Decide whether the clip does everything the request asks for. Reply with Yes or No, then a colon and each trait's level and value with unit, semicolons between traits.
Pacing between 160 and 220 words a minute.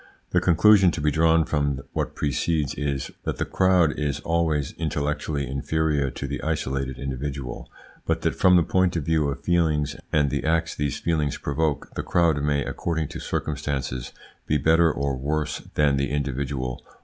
Yes: average, 175 wpm